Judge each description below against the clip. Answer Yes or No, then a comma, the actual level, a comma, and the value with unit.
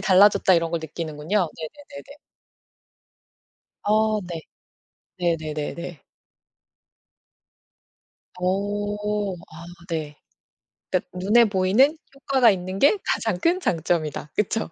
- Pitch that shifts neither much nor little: Yes, average, 4.3 semitones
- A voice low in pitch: No, medium, 185 Hz